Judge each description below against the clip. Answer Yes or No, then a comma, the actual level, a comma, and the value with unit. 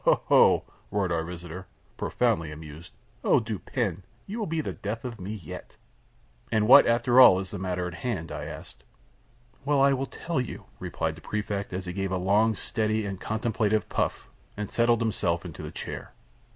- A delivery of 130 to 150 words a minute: No, average, 190 wpm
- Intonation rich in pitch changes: No, average, 4.5 semitones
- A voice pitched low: Yes, low, 100 Hz